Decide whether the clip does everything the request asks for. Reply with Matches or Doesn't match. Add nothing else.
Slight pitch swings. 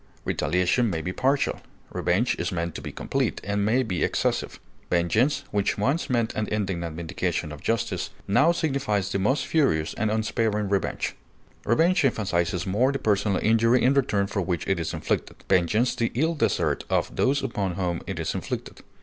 Doesn't match